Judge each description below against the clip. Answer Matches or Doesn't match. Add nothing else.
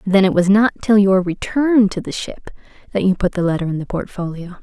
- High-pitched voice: Matches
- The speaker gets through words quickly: Matches